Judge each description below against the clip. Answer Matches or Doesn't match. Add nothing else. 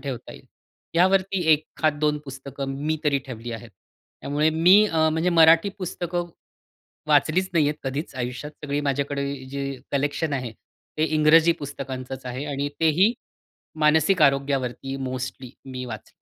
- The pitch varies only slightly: Doesn't match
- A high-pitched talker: Doesn't match